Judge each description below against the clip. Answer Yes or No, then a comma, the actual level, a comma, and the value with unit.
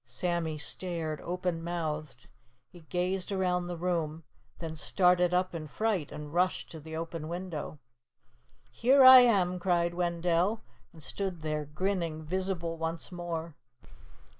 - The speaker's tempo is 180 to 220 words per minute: No, slow, 135 wpm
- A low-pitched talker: No, medium, 175 Hz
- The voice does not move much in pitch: Yes, narrow, 2.3 semitones